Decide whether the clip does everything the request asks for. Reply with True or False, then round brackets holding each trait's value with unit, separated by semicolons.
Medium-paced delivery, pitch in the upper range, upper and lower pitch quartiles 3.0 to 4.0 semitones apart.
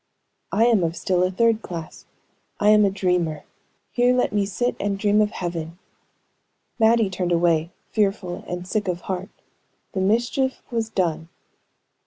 True (155 wpm; 195 Hz; 3.7 semitones)